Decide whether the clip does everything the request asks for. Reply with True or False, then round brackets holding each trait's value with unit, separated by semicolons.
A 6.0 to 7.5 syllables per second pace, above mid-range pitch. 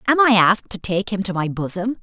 True (6.4 syllables/s; 205 Hz)